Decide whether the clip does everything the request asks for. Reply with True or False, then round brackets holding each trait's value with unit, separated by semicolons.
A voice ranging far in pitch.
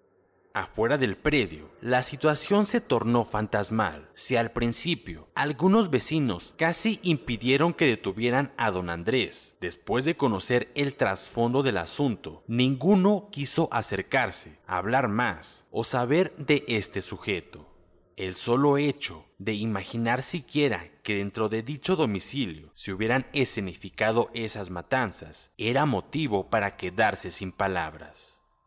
True (6.5 semitones)